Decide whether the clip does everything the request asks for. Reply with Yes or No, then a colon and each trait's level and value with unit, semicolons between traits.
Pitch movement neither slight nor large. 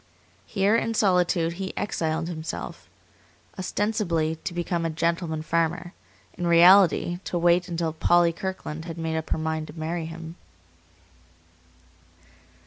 No: narrow, 1.8 semitones